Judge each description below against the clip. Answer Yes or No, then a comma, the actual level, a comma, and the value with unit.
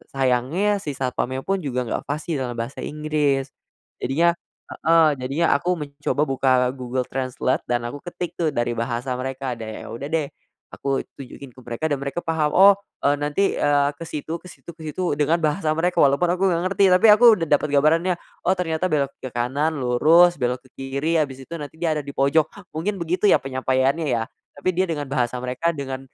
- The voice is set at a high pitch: No, medium, 145 Hz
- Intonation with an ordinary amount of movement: Yes, average, 4.0 semitones